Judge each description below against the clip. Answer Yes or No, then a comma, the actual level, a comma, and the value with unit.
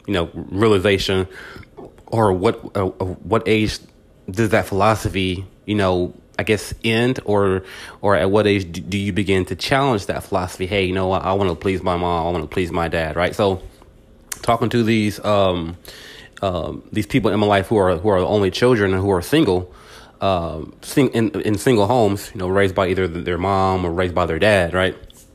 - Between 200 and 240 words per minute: Yes, fast, 205 wpm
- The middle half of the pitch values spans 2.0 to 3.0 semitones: Yes, narrow, 2.6 semitones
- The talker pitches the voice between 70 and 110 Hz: Yes, very low, 95 Hz